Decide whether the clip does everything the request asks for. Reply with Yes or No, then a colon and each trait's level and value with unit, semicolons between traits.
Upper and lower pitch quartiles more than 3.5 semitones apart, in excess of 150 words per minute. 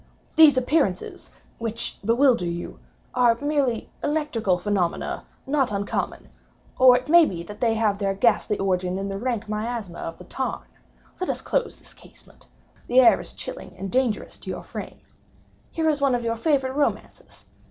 Yes: average, 5.2 semitones; average, 160 wpm